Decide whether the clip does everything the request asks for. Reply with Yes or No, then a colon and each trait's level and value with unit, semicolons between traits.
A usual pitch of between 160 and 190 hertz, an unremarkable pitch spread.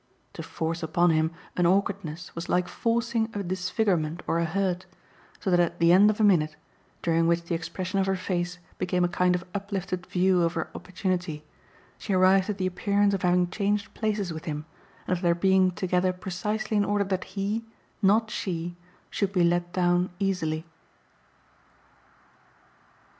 No: medium, 185 Hz; narrow, 2.2 semitones